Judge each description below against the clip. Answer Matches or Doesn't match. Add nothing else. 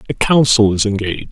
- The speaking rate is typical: Matches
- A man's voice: Matches